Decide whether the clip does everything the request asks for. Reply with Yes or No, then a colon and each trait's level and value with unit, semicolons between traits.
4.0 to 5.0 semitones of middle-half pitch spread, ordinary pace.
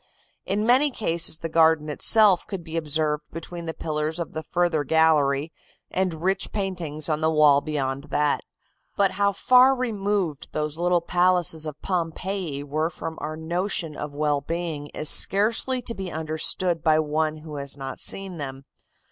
No: average, 3.3 semitones; average, 165 wpm